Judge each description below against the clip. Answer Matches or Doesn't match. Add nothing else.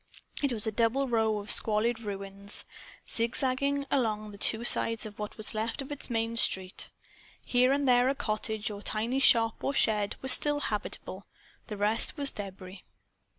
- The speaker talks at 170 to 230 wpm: Matches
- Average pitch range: Matches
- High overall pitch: Matches